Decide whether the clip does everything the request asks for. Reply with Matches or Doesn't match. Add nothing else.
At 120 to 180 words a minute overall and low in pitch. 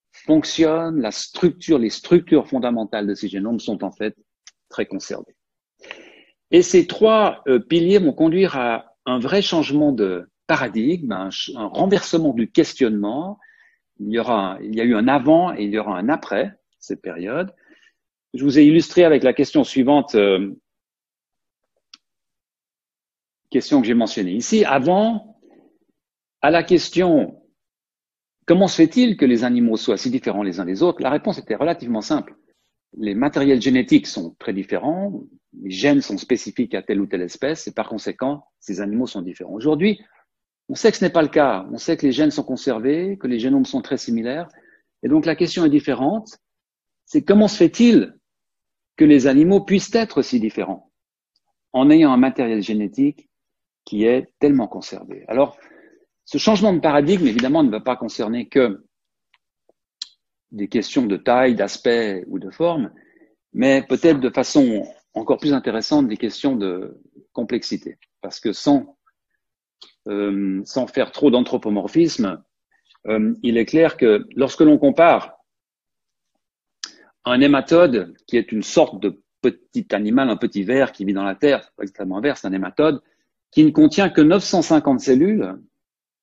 Doesn't match